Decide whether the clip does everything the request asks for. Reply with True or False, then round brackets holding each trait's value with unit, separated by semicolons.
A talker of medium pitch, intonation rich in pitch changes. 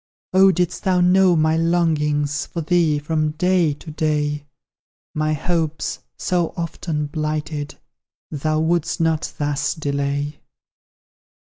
False (155 Hz; 2.4 semitones)